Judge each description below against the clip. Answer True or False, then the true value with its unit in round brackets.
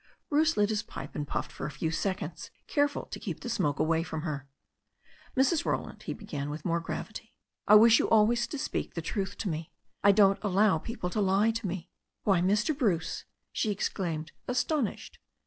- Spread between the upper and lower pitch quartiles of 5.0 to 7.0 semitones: True (5.3 semitones)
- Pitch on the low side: False (200 Hz)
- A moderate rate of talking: True (190 wpm)